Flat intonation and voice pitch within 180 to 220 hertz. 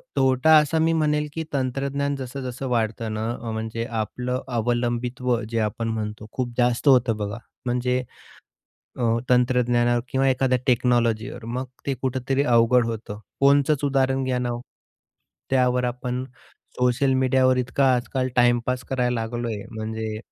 No: narrow, 2.1 semitones; low, 125 Hz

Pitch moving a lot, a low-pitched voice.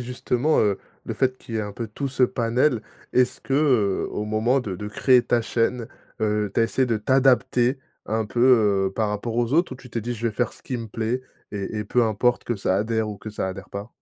No: average, 3.0 semitones; low, 115 Hz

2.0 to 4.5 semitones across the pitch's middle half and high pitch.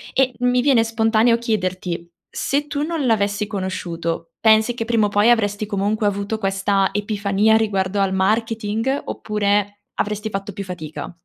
Yes: narrow, 2.5 semitones; high, 210 Hz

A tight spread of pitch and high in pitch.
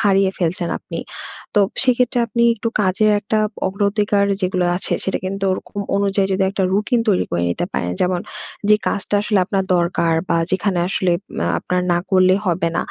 Yes: narrow, 2.2 semitones; high, 195 Hz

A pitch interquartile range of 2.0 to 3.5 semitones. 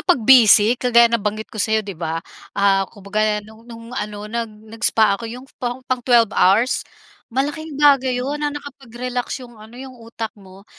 Yes: average, 3.1 semitones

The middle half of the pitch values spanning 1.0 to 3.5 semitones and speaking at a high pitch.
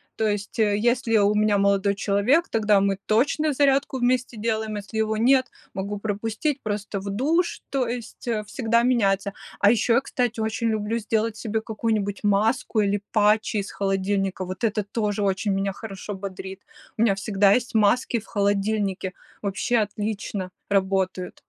Yes: narrow, 2.4 semitones; high, 210 Hz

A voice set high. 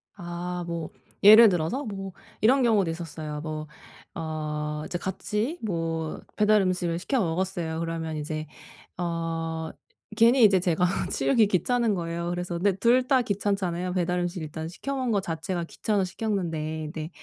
No: medium, 175 Hz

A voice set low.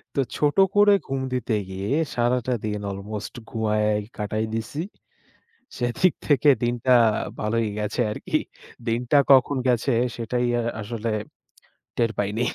Yes: low, 115 Hz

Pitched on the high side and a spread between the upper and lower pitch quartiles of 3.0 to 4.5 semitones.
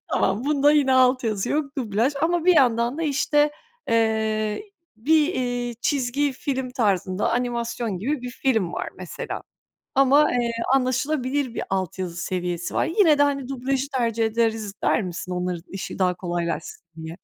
No: high, 245 Hz; average, 5.0 semitones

